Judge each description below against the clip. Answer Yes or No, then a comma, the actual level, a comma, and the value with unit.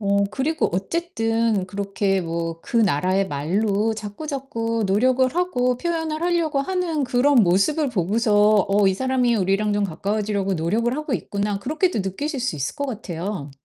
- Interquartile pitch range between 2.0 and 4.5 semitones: No, wide, 5.5 semitones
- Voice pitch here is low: No, high, 215 Hz